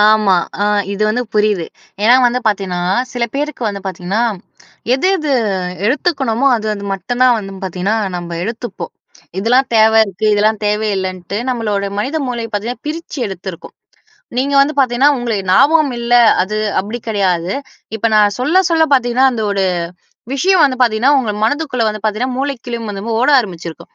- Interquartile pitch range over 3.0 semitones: Yes, average, 4.2 semitones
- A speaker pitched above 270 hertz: No, high, 225 Hz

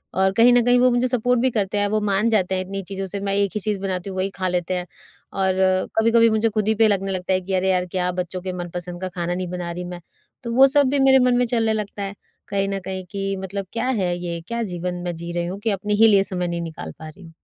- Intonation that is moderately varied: Yes, average, 3.3 semitones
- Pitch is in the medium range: No, high, 195 Hz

